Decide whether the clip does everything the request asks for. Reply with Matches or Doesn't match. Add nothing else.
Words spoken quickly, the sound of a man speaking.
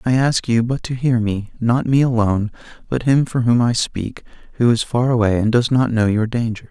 Matches